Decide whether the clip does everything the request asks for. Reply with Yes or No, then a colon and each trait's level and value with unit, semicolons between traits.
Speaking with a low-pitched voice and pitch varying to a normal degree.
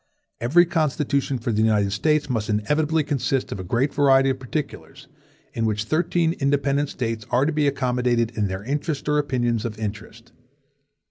Yes: low, 130 Hz; average, 4.6 semitones